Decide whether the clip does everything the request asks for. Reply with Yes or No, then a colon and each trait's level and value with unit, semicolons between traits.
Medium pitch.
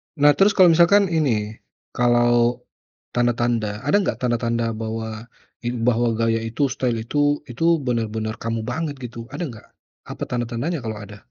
No: low, 120 Hz